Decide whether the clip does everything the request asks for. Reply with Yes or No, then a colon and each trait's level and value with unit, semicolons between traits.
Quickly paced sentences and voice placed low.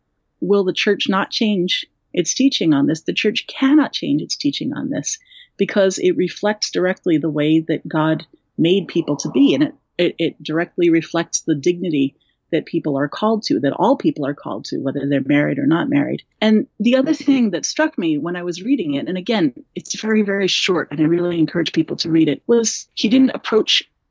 No: fast, 210 wpm; high, 195 Hz